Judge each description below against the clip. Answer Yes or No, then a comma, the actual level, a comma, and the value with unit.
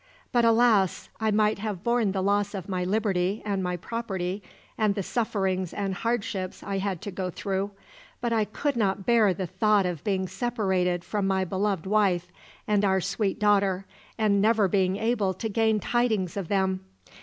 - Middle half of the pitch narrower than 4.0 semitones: Yes, narrow, 2.4 semitones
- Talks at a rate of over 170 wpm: Yes, average, 180 wpm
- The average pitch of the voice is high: Yes, high, 200 Hz